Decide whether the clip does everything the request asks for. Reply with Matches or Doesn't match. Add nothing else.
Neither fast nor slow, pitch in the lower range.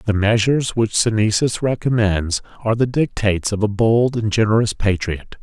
Matches